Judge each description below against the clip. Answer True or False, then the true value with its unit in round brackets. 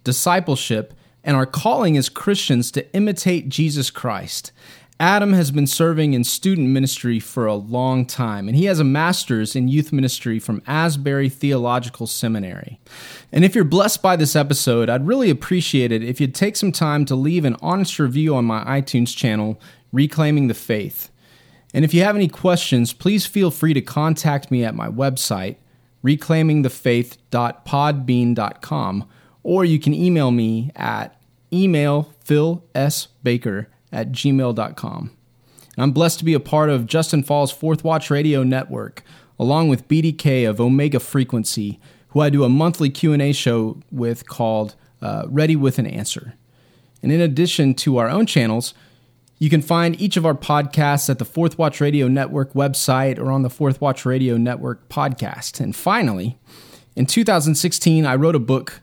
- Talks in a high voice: False (140 Hz)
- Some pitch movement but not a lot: True (4.2 semitones)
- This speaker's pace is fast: False (160 wpm)